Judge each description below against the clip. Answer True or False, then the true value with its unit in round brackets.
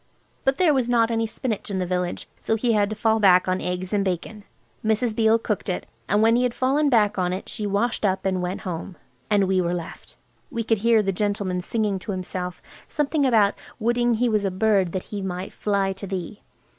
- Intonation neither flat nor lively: True (3.4 semitones)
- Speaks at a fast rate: True (220 wpm)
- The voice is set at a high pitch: True (205 Hz)